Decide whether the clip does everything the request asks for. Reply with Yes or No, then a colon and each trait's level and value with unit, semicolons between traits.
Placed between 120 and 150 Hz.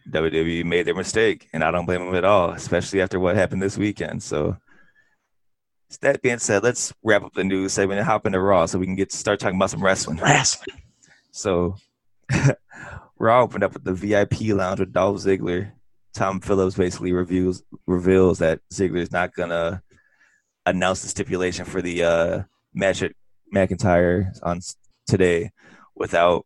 No: very low, 95 Hz